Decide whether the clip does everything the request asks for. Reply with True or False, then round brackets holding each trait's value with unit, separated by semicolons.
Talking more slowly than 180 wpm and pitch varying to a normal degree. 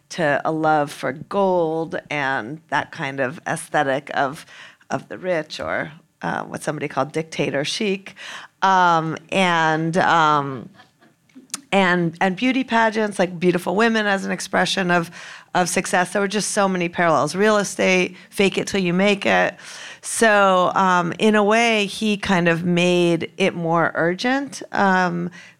True (150 wpm; 3.3 semitones)